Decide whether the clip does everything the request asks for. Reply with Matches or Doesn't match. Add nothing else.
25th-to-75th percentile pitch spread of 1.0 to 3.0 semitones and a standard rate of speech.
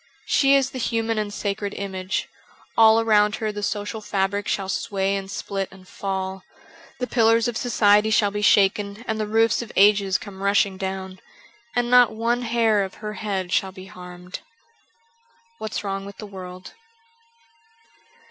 Matches